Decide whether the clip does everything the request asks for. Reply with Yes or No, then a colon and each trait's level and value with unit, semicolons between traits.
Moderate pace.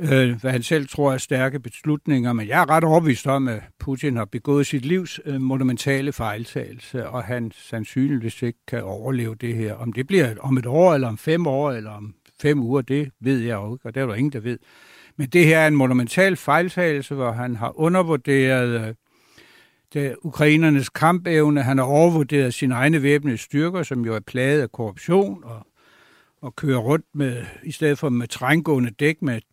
Yes: average, 190 wpm